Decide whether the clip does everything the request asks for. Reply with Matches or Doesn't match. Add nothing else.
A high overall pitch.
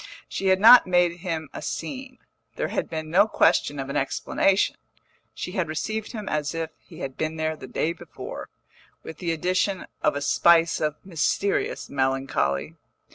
Doesn't match